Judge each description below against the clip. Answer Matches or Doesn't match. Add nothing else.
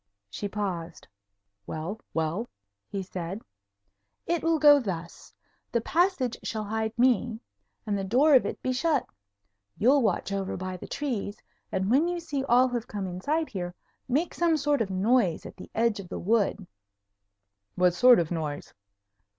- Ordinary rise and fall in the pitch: Doesn't match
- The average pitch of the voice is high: Matches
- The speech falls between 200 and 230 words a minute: Doesn't match